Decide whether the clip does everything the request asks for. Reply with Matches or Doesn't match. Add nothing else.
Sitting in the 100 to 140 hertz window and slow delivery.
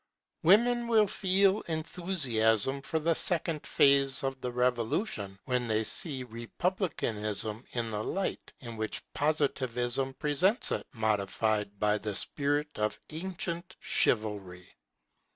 Matches